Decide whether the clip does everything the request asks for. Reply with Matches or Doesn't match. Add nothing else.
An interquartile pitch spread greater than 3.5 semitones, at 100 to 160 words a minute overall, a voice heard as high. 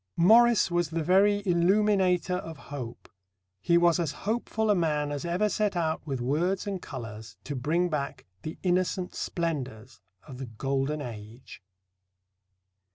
Doesn't match